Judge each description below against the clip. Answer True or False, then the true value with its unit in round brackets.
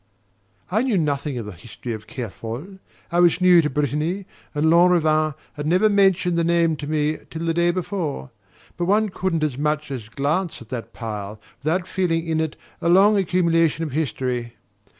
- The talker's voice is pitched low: False (160 Hz)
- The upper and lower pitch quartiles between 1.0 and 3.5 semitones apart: False (4.0 semitones)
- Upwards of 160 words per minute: True (180 wpm)